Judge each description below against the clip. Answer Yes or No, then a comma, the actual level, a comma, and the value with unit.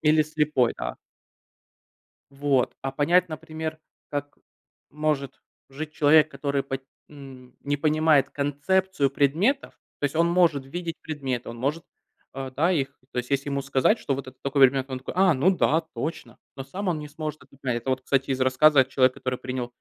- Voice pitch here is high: No, medium, 145 Hz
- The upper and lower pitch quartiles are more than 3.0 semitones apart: No, average, 2.7 semitones